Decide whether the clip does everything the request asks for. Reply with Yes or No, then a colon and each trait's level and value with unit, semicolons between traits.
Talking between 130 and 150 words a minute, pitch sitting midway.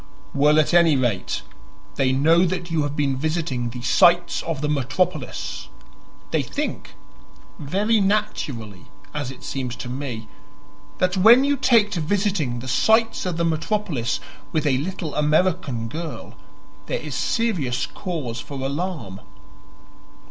Yes: average, 140 wpm; medium, 155 Hz